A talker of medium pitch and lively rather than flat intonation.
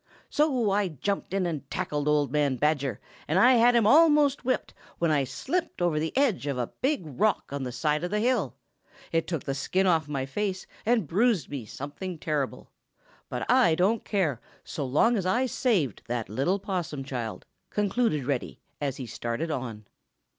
Yes: medium, 165 Hz; wide, 7.1 semitones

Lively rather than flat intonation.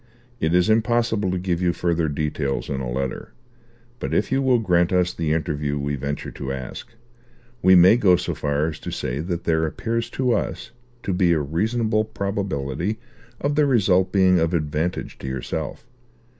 Yes: wide, 5.8 semitones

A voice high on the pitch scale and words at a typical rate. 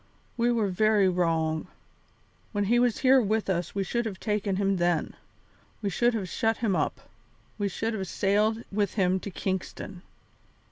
Yes: high, 200 Hz; average, 170 wpm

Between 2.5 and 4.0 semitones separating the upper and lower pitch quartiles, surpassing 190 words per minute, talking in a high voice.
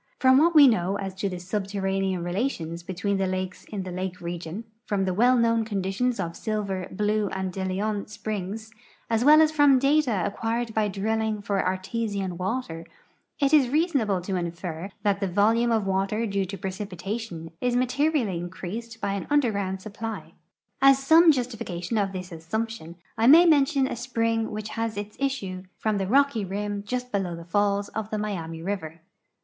No: average, 3.7 semitones; average, 175 wpm; high, 205 Hz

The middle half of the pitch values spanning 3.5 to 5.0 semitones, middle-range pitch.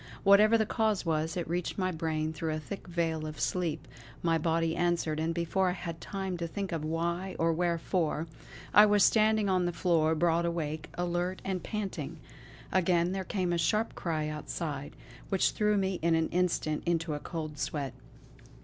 No: average, 2.7 semitones; medium, 170 Hz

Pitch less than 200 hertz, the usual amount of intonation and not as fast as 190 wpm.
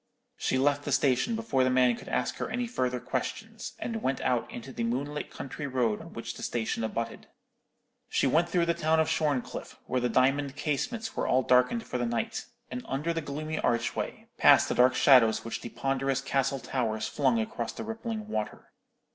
No: low, 135 Hz; average, 4.0 semitones; average, 195 wpm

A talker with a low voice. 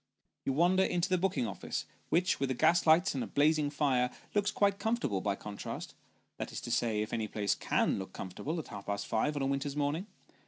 No: medium, 145 Hz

